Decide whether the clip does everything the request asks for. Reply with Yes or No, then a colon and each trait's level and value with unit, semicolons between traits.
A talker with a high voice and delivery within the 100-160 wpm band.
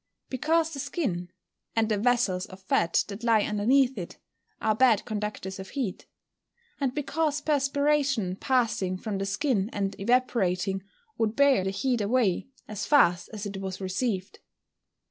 Yes: high, 215 Hz; average, 150 wpm